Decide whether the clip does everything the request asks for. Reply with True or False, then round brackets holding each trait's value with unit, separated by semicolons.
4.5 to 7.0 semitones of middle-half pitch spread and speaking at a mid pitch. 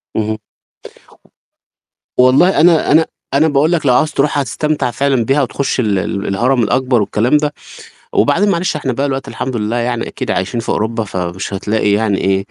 False (5.2 semitones; 125 Hz)